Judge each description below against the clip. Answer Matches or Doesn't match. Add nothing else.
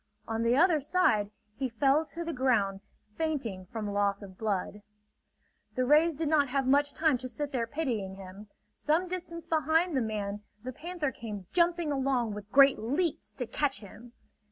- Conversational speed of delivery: Matches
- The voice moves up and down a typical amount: Doesn't match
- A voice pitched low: Doesn't match